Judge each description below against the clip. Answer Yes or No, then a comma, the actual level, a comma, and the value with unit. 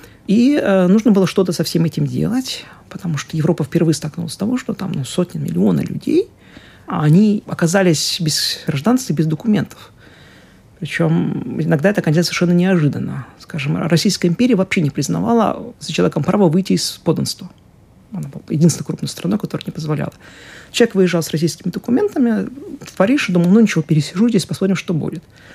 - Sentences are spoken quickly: Yes, fast, 170 wpm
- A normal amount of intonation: Yes, average, 4.1 semitones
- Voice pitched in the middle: Yes, medium, 175 Hz